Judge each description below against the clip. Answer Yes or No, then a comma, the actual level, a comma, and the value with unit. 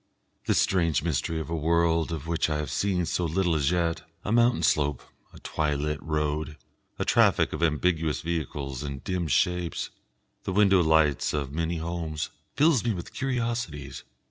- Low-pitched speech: Yes, very low, 80 Hz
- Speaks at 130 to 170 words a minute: Yes, average, 165 wpm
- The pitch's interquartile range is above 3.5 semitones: No, average, 2.9 semitones